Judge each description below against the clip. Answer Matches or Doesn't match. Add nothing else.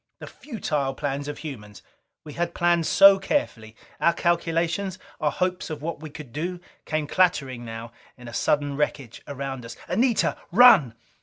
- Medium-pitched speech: Matches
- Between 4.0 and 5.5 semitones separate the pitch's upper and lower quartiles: Matches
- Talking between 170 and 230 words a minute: Doesn't match